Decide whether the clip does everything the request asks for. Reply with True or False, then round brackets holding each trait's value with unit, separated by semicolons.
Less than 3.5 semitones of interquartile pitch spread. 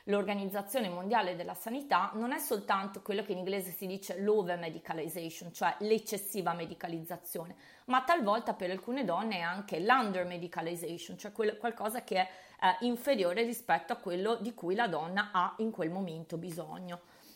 False (4.0 semitones)